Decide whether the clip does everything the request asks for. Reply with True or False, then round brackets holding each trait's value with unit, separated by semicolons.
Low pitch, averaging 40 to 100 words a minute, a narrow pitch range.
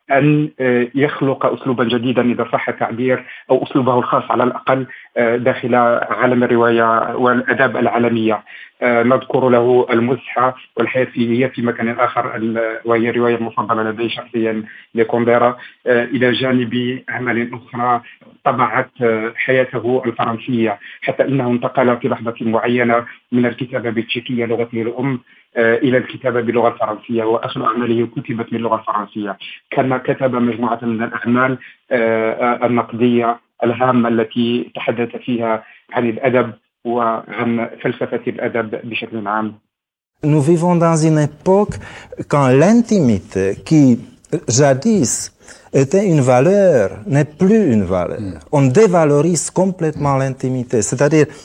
False (120 Hz; 110 wpm; 2.0 semitones)